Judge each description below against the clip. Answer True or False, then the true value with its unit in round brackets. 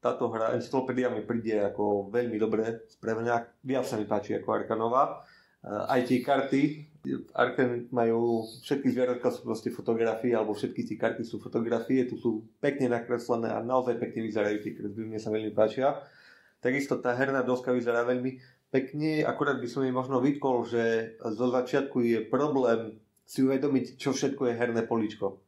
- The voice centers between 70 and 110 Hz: False (120 Hz)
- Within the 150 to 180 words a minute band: True (160 wpm)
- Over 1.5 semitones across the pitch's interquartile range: True (2.5 semitones)